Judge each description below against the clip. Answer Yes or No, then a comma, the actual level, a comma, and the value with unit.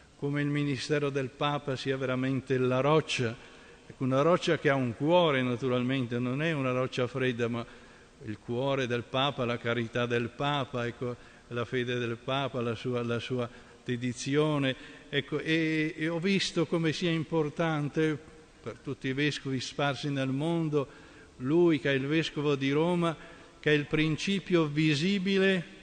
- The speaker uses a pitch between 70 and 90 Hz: No, medium, 140 Hz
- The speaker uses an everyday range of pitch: Yes, average, 3.9 semitones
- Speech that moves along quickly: No, average, 155 wpm